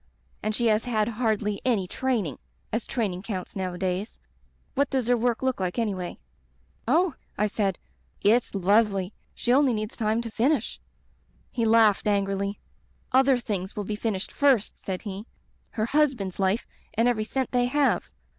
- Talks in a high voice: Yes, high, 215 Hz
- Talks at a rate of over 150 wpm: Yes, average, 165 wpm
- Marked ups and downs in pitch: No, average, 3.8 semitones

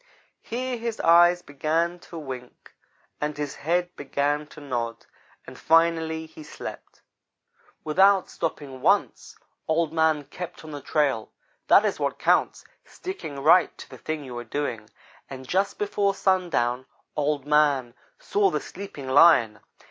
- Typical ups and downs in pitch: Yes, average, 3.9 semitones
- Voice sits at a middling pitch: Yes, medium, 155 Hz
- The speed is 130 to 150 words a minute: Yes, average, 140 wpm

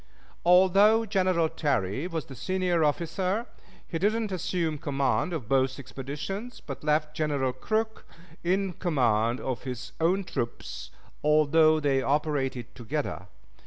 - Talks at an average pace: No, slow, 125 wpm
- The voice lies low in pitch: No, medium, 155 Hz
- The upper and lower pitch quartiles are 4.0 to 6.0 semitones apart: Yes, wide, 5.6 semitones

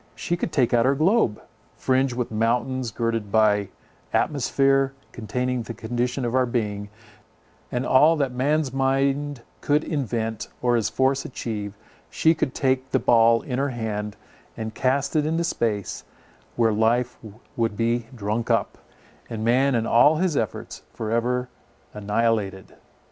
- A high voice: No, low, 120 Hz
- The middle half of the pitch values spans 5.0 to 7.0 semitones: No, average, 3.3 semitones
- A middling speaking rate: Yes, average, 150 wpm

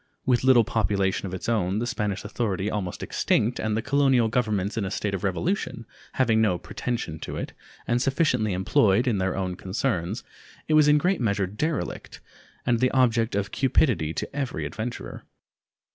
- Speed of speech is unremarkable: Yes, average, 175 wpm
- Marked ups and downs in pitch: No, average, 4.5 semitones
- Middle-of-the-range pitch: No, low, 110 Hz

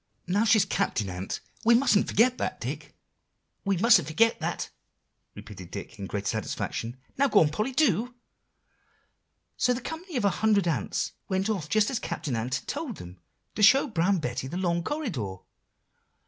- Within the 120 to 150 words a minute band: No, average, 170 wpm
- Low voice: No, high, 195 Hz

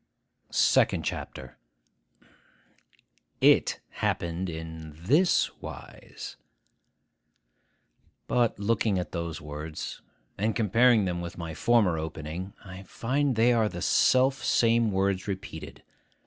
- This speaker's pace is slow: Yes, slow, 105 wpm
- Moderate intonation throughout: No, wide, 5.7 semitones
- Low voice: Yes, very low, 95 Hz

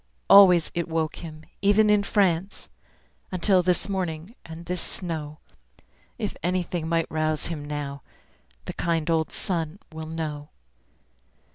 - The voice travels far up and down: No, average, 2.7 semitones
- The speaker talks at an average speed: No, slow, 130 wpm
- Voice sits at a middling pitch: Yes, medium, 165 Hz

